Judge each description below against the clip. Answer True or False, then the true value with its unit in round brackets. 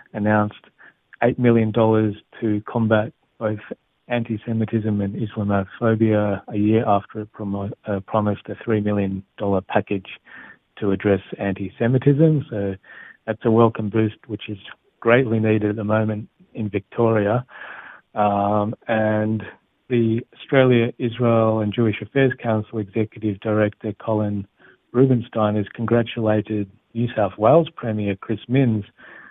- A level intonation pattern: True (1.9 semitones)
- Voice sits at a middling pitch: False (110 Hz)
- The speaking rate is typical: True (125 wpm)